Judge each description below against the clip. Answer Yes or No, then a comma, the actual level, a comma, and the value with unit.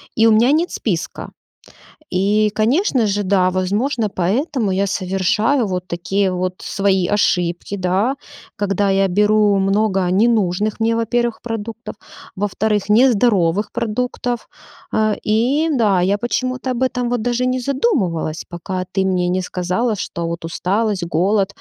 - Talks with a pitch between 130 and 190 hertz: No, high, 205 Hz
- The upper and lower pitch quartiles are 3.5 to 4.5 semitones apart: Yes, average, 4.0 semitones